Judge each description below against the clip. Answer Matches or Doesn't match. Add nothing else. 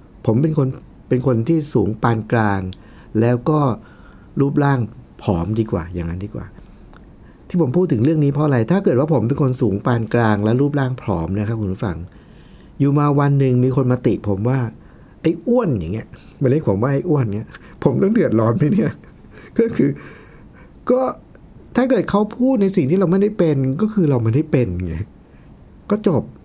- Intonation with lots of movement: Matches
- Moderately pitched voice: Doesn't match